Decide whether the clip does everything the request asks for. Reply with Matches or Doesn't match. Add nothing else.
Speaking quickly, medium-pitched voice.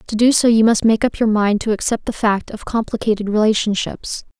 Doesn't match